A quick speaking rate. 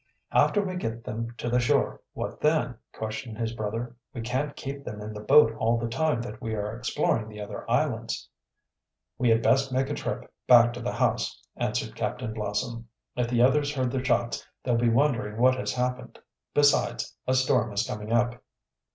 No: average, 190 wpm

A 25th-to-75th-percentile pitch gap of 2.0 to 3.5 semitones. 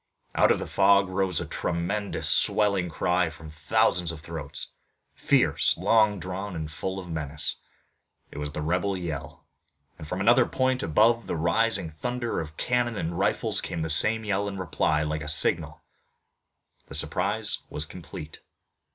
No: average, 4.6 semitones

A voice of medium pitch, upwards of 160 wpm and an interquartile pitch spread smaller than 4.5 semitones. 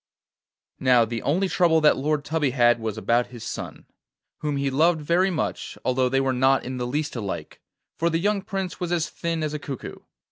No: medium, 145 Hz; fast, 205 wpm; average, 4.8 semitones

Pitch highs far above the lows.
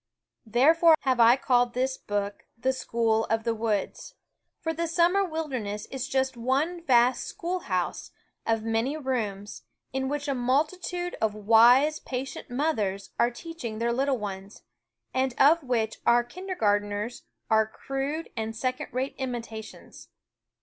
No: average, 4.3 semitones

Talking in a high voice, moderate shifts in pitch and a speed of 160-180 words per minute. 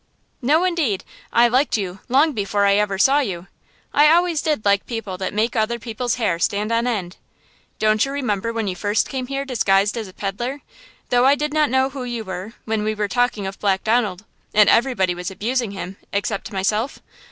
No: high, 220 Hz; average, 4.3 semitones; average, 200 wpm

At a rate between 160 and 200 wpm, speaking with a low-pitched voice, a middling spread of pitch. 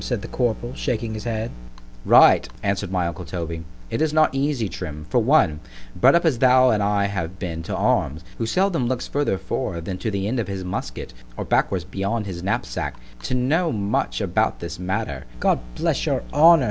No: average, 195 wpm; low, 105 Hz; wide, 5.9 semitones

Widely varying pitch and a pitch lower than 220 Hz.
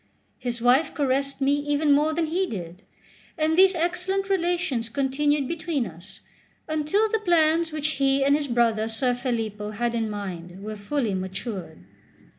No: wide, 6.1 semitones; very high, 275 Hz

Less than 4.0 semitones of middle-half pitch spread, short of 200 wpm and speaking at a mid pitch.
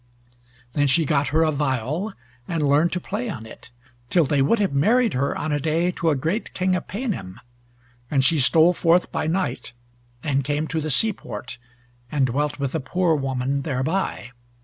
No: average, 4.5 semitones; average, 190 wpm; medium, 155 Hz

